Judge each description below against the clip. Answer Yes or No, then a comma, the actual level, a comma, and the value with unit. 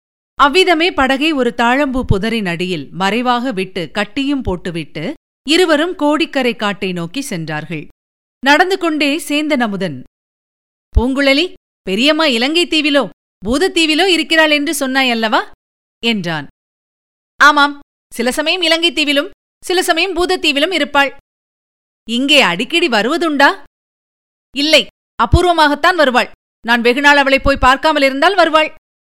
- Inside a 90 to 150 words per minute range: Yes, average, 95 wpm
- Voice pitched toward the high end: Yes, very high, 280 Hz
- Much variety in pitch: No, average, 5.0 semitones